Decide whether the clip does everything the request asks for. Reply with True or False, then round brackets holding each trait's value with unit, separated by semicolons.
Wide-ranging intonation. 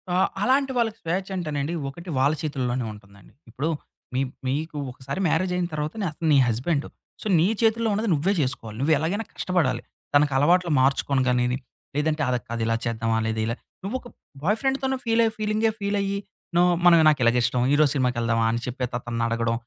True (7.1 semitones)